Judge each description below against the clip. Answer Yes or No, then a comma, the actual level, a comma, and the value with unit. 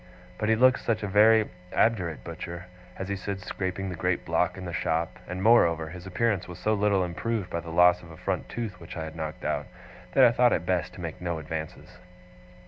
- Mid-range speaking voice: No, very low, 90 Hz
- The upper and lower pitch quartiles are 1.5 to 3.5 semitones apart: No, average, 4.0 semitones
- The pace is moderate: No, fast, 220 wpm